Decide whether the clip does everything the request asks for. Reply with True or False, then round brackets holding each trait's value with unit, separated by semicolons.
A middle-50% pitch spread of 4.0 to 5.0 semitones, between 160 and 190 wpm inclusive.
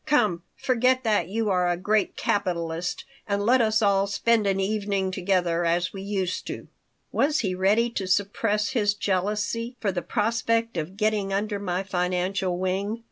False (2.8 semitones; 165 wpm)